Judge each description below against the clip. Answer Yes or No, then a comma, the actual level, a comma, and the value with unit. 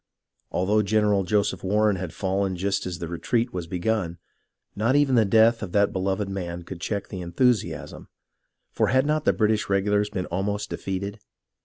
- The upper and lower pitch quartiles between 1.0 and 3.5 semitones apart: Yes, narrow, 2.5 semitones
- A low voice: Yes, low, 100 Hz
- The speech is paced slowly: No, average, 175 wpm